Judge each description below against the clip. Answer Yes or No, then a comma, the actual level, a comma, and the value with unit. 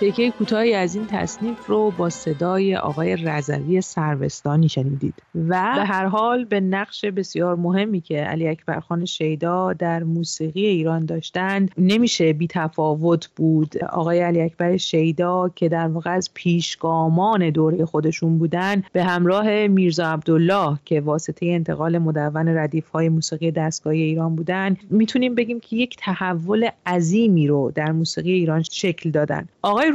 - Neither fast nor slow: Yes, average, 145 wpm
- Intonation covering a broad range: No, average, 3.2 semitones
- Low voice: No, medium, 170 Hz